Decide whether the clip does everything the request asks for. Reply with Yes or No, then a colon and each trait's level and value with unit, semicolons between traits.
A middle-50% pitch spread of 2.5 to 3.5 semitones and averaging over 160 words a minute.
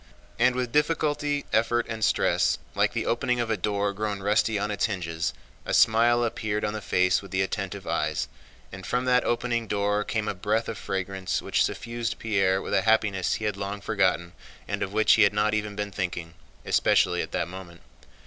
Yes: average, 2.8 semitones; average, 195 wpm